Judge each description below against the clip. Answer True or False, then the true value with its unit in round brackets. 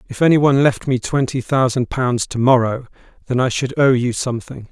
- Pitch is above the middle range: False (125 Hz)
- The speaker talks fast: False (190 wpm)